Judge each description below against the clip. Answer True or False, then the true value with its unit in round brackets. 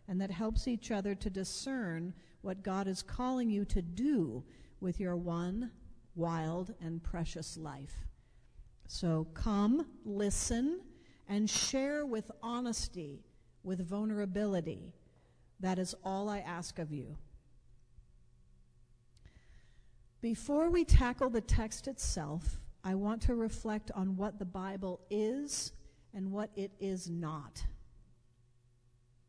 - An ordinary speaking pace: False (115 wpm)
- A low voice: False (190 Hz)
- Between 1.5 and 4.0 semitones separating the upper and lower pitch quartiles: False (4.9 semitones)